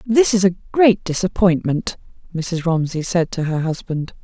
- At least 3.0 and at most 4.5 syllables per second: Yes, 4.3 syllables/s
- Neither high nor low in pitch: Yes, medium, 180 Hz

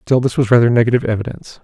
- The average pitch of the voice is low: Yes, low, 120 Hz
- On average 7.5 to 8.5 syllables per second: Yes, 8.2 syllables/s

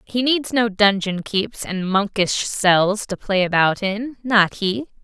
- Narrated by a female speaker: Yes, female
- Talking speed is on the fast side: No, average, 155 wpm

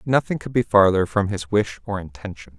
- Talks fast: Yes, fast, 210 wpm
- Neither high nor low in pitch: No, low, 100 Hz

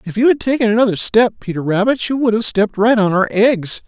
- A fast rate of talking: Yes, fast, 250 wpm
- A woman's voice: No, male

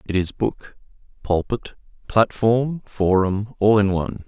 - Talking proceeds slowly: Yes, slow, 125 wpm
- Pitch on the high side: No, low, 105 Hz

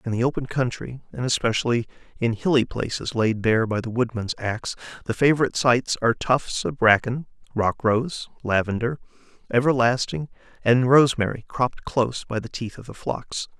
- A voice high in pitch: No, low, 120 Hz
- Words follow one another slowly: No, average, 165 wpm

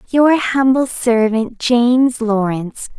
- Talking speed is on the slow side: Yes, slow, 100 wpm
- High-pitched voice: Yes, high, 240 Hz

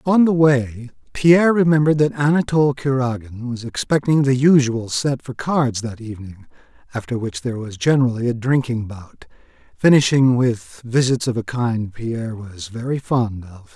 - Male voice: Yes, male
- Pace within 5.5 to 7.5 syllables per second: No, 4.9 syllables/s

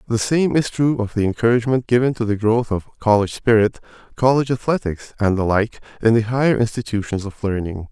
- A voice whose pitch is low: Yes, low, 115 Hz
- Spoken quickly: No, average, 190 wpm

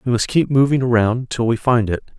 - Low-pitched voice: Yes, low, 120 Hz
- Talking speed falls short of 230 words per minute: No, fast, 250 wpm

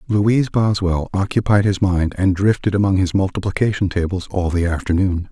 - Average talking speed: Yes, average, 160 wpm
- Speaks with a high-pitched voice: No, very low, 95 Hz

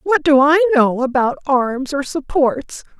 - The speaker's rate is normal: Yes, average, 160 wpm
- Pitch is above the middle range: Yes, very high, 285 Hz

